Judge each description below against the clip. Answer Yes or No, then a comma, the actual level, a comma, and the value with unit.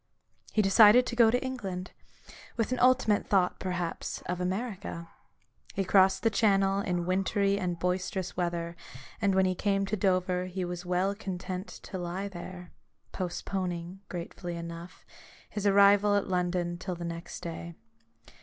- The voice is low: No, medium, 185 Hz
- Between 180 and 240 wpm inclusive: No, average, 150 wpm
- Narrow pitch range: Yes, narrow, 2.2 semitones